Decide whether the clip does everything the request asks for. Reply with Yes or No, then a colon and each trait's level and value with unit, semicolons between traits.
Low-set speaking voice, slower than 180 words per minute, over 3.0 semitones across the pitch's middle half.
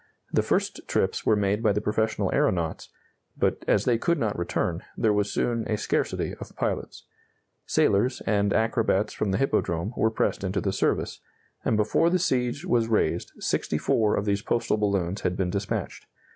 No: low, 105 Hz; average, 170 wpm; narrow, 2.4 semitones